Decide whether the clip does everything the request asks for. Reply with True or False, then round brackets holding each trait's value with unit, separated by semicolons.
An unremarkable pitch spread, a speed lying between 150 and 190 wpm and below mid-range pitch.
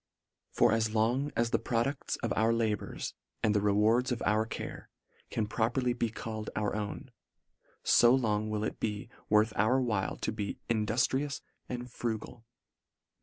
False (2.2 semitones; 160 wpm; 110 Hz)